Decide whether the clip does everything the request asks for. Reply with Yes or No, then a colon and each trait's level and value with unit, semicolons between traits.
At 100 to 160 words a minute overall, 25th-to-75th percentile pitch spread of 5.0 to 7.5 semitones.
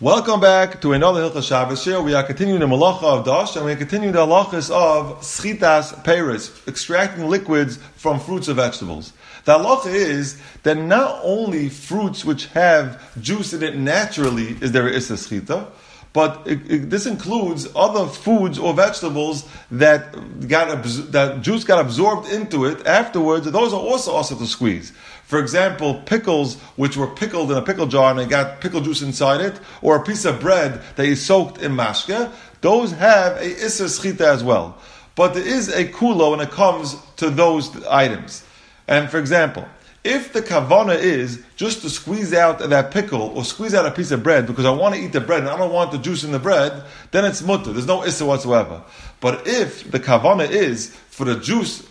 No: average, 195 wpm; wide, 5.5 semitones